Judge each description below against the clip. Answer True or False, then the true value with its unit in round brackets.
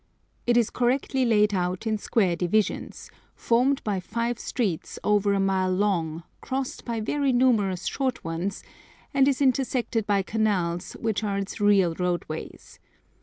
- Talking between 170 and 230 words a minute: False (145 wpm)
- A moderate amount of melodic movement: True (4.5 semitones)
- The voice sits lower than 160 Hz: False (210 Hz)